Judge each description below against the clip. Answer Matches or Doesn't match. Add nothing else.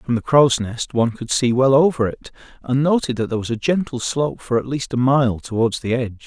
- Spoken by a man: Matches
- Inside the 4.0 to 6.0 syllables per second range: Matches